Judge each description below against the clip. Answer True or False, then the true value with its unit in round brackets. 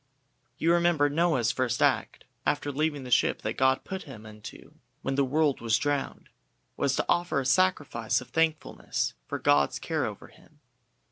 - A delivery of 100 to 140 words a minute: False (165 wpm)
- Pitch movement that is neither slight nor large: True (4.2 semitones)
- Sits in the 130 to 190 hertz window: True (140 Hz)